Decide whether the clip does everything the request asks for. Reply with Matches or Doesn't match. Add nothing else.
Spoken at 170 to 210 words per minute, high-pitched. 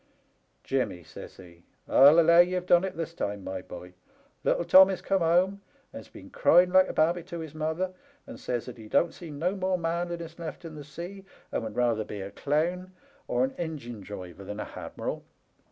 Doesn't match